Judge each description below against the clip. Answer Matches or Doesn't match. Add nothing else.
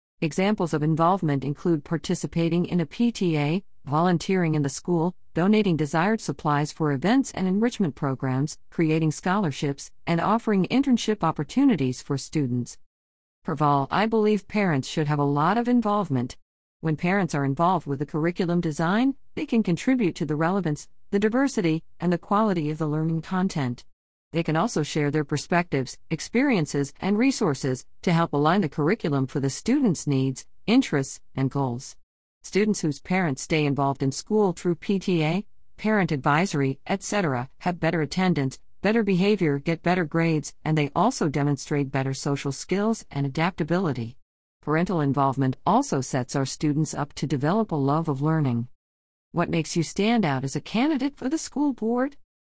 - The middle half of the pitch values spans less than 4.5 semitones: Doesn't match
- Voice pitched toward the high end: Doesn't match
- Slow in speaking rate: Doesn't match